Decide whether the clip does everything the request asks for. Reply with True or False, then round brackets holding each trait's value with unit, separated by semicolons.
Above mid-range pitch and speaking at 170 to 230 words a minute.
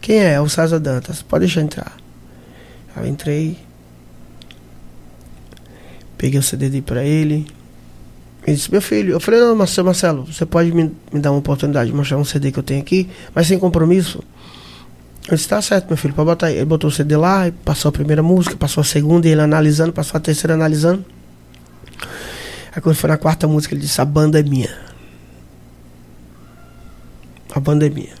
False (150 Hz; 185 wpm)